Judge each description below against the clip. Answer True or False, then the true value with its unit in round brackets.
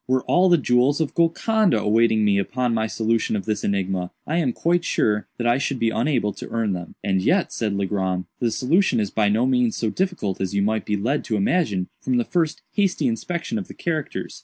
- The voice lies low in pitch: True (115 Hz)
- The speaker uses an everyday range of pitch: False (7.2 semitones)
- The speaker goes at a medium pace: False (220 wpm)